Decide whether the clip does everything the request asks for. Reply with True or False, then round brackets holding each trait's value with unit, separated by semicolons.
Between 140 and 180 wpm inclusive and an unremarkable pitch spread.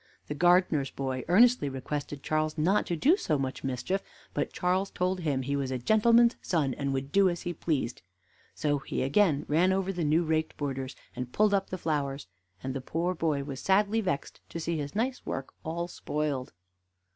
False (190 wpm; 5.0 semitones)